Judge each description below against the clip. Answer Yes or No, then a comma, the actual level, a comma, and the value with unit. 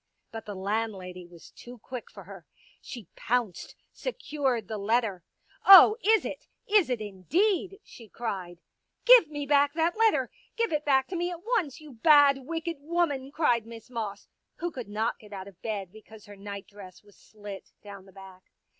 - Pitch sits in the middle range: No, high, 235 Hz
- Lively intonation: Yes, wide, 7.4 semitones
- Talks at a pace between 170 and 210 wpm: Yes, average, 190 wpm